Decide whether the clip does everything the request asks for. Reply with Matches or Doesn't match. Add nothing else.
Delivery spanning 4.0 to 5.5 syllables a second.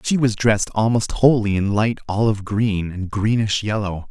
Matches